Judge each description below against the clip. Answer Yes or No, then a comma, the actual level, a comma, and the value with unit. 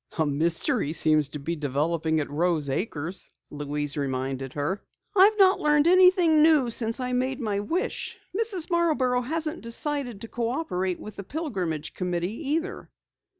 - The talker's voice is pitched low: No, high, 220 Hz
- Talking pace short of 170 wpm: Yes, average, 150 wpm